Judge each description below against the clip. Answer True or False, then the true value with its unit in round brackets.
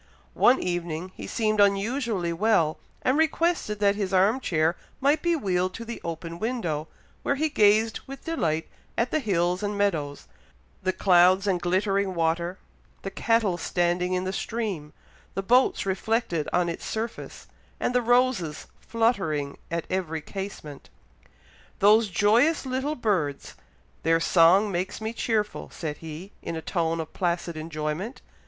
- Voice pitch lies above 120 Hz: True (190 Hz)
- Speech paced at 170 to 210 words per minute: False (150 wpm)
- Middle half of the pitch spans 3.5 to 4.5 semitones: False (5.0 semitones)